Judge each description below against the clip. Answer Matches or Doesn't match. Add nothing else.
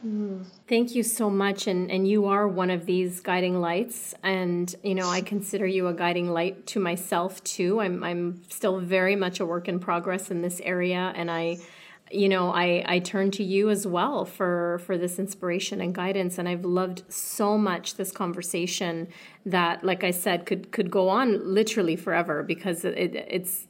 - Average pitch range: Doesn't match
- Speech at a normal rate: Matches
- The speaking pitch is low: Doesn't match